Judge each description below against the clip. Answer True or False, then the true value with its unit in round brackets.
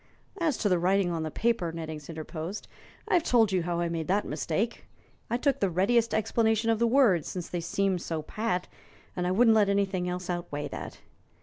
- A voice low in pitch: False (185 Hz)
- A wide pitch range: False (4.6 semitones)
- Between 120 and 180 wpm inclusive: False (200 wpm)